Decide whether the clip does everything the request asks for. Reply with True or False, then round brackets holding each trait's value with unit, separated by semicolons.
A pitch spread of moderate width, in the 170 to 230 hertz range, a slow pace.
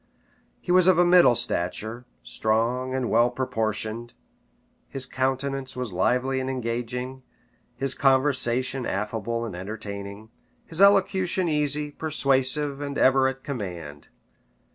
False (3.6 semitones; 130 Hz; 120 wpm)